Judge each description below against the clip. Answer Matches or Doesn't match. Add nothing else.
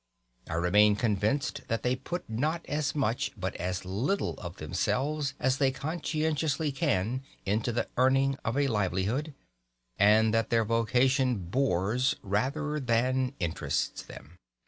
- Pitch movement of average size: Matches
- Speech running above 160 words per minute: Doesn't match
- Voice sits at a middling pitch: Doesn't match